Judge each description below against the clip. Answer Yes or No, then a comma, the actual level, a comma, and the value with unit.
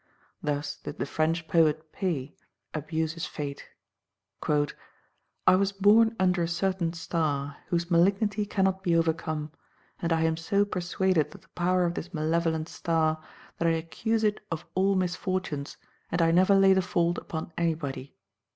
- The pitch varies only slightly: No, average, 3.0 semitones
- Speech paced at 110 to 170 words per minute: Yes, average, 155 wpm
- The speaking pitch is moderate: Yes, medium, 170 Hz